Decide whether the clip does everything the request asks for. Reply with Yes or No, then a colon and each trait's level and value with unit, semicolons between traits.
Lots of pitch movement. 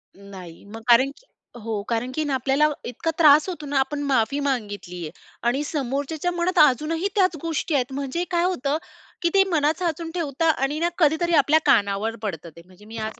Yes: wide, 6.2 semitones